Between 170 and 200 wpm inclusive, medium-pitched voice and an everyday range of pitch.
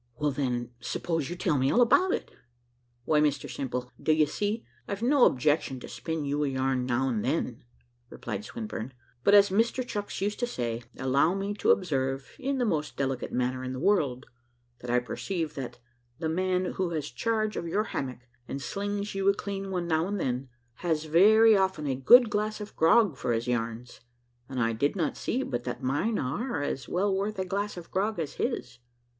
No: average, 195 wpm; medium, 160 Hz; wide, 7.6 semitones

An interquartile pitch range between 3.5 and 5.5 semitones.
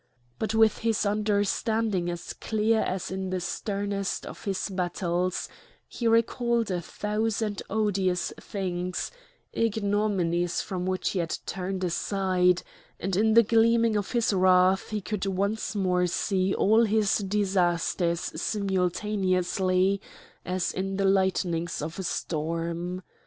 No: average, 2.7 semitones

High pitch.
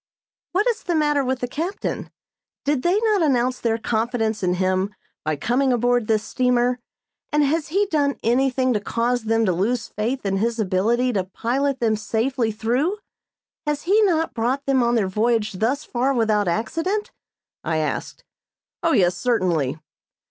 Yes: high, 245 Hz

